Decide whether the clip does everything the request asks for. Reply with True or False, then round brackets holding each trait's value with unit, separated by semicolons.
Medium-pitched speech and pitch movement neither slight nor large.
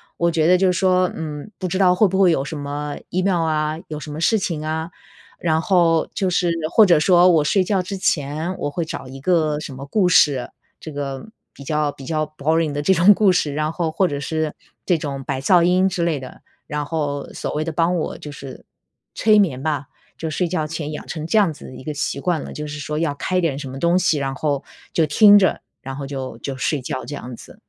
True (155 Hz; 3.7 semitones)